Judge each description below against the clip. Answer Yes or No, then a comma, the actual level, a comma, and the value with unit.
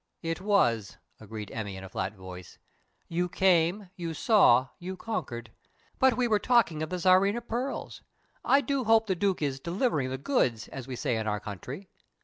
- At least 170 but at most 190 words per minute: Yes, average, 180 wpm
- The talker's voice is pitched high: No, medium, 170 Hz